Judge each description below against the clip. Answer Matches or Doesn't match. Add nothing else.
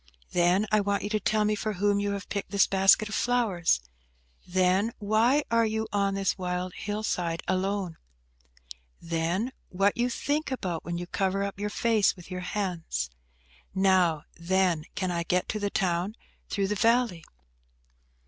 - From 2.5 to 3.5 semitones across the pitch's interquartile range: Matches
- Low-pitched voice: Doesn't match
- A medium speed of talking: Matches